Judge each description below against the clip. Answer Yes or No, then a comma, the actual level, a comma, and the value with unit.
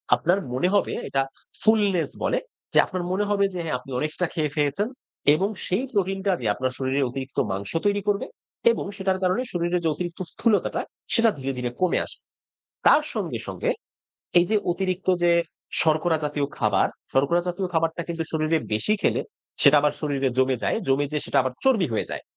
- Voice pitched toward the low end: No, medium, 170 Hz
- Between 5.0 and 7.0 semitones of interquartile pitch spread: Yes, average, 5.3 semitones